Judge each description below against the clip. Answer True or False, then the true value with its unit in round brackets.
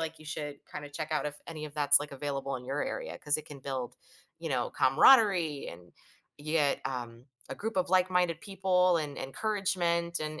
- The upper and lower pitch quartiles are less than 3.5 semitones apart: False (4.1 semitones)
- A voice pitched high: False (155 Hz)